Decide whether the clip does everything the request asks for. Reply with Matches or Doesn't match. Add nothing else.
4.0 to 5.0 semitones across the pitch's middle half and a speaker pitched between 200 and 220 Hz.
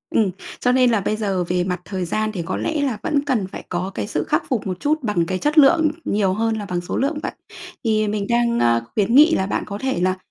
Doesn't match